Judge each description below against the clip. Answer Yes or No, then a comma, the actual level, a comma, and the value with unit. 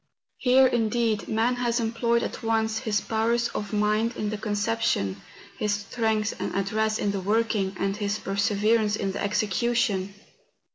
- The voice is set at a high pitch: Yes, high, 215 Hz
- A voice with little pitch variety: Yes, narrow, 2.1 semitones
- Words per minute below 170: Yes, average, 155 wpm